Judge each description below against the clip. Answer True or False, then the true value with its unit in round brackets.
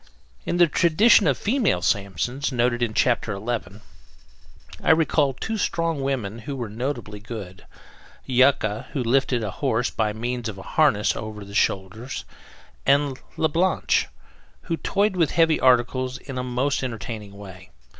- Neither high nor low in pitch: False (125 Hz)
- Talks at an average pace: True (155 wpm)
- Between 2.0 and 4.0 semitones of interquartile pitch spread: False (5.0 semitones)